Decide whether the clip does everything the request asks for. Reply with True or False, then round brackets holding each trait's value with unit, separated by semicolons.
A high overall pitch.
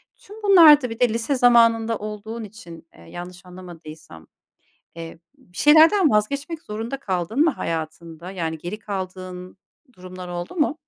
True (205 Hz)